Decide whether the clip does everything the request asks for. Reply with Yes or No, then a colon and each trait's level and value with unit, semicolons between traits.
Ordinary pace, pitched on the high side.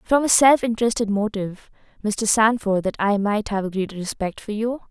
Yes: average, 185 wpm; high, 215 Hz